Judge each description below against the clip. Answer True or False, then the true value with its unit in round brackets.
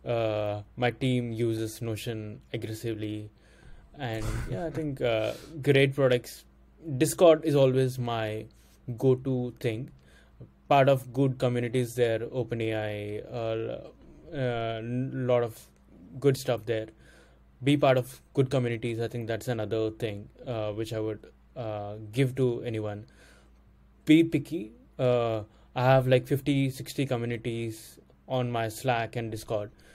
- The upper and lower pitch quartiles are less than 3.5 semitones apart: True (3.1 semitones)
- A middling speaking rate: False (130 wpm)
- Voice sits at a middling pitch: False (120 Hz)